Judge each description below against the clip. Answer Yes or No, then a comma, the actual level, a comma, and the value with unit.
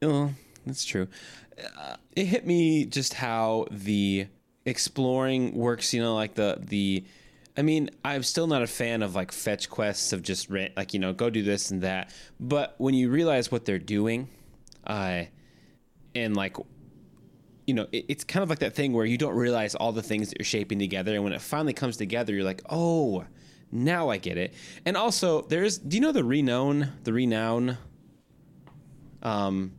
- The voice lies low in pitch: Yes, low, 120 Hz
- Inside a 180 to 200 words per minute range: Yes, average, 185 wpm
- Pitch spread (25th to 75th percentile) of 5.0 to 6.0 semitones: Yes, wide, 5.6 semitones